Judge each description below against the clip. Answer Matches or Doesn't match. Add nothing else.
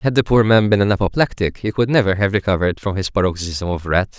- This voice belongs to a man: Matches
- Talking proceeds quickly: Matches